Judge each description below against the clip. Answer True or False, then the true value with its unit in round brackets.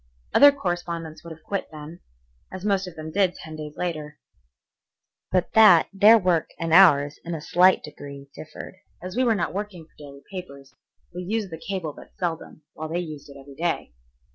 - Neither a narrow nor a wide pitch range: True (3.4 semitones)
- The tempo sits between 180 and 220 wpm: True (190 wpm)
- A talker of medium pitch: True (170 Hz)